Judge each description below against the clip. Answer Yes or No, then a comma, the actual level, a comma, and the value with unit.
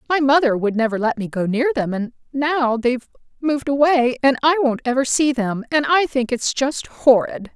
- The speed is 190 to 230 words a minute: Yes, fast, 205 wpm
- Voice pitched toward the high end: Yes, very high, 260 Hz